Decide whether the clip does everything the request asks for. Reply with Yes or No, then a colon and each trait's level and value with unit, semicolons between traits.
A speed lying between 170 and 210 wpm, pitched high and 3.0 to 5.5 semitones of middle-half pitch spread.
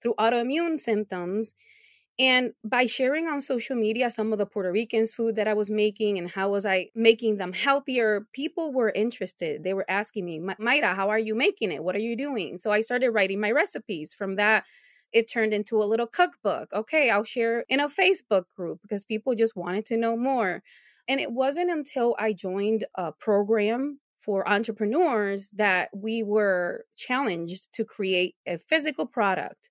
Yes: average, 180 wpm; high, 220 Hz; average, 3.9 semitones